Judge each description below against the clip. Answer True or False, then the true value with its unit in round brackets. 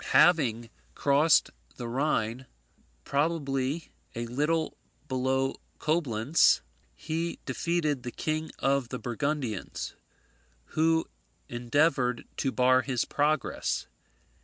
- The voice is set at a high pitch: False (135 Hz)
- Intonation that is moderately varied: True (3.9 semitones)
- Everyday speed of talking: False (90 wpm)